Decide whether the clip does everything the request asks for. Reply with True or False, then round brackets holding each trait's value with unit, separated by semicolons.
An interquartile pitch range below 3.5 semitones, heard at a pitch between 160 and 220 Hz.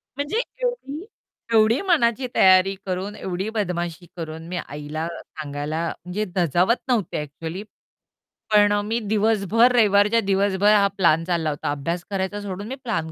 False (4.4 semitones; 195 Hz)